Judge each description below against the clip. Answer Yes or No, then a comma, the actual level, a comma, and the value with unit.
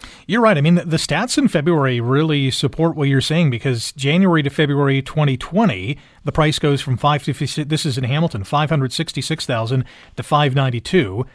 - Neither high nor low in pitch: Yes, medium, 145 Hz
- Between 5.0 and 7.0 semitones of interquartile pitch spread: No, average, 3.2 semitones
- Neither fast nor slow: Yes, average, 165 wpm